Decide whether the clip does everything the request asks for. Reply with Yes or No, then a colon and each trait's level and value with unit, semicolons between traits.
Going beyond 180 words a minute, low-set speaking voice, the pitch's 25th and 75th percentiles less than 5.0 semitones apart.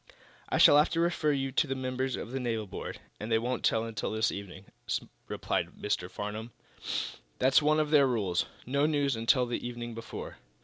Yes: average, 190 wpm; low, 125 Hz; average, 3.9 semitones